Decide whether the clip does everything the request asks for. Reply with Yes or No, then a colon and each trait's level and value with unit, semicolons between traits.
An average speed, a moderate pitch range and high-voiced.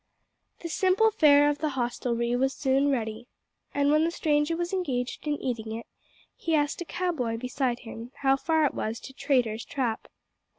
Yes: average, 180 wpm; average, 4.2 semitones; very high, 270 Hz